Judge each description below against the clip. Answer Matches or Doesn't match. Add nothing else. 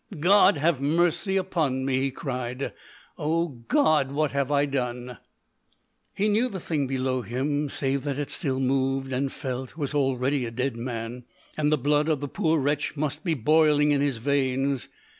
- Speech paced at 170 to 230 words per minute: Matches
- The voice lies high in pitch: Doesn't match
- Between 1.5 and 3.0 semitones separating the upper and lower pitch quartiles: Matches